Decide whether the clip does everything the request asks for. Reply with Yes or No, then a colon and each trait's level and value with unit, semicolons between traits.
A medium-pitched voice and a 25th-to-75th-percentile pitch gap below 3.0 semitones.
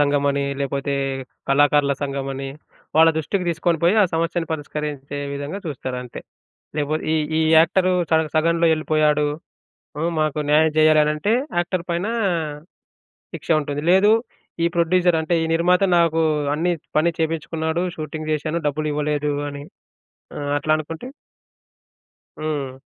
Yes: medium, 155 Hz; narrow, 2.4 semitones